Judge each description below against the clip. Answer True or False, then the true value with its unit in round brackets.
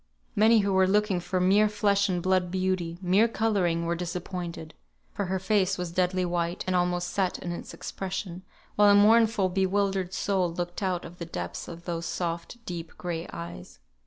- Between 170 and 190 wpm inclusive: True (180 wpm)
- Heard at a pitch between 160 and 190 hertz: True (185 Hz)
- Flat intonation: True (2.3 semitones)